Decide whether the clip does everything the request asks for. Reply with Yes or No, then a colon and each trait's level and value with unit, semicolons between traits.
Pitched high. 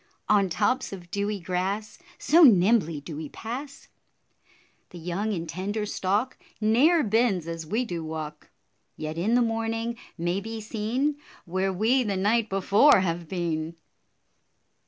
Yes: high, 200 Hz